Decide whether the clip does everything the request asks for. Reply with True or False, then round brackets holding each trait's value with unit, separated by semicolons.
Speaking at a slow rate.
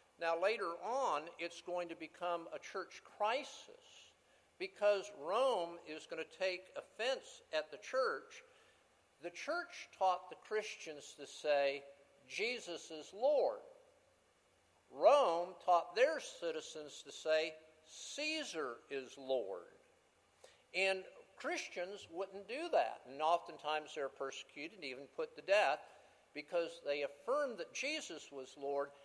True (125 wpm)